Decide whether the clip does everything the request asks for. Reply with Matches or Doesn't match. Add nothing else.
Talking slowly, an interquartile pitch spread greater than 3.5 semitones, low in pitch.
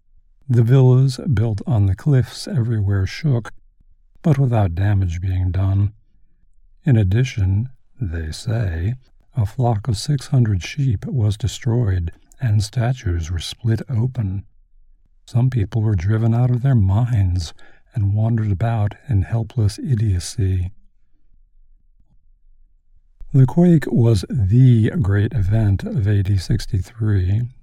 Matches